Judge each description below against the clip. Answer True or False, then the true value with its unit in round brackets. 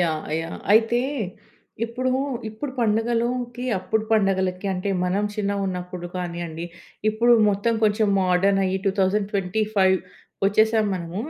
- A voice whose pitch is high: True (200 Hz)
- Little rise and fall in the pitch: False (3.1 semitones)